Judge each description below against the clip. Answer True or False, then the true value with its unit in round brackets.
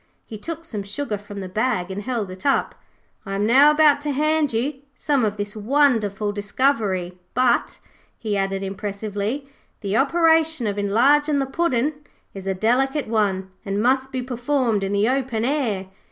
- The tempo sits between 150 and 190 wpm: True (170 wpm)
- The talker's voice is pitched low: False (230 Hz)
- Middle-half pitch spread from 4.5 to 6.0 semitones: True (5.6 semitones)